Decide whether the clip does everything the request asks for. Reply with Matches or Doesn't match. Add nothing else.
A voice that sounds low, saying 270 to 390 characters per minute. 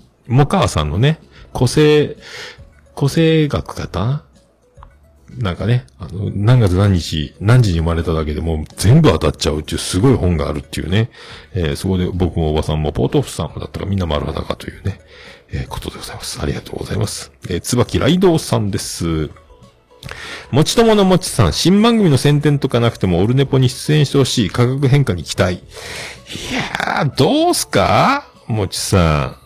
Matches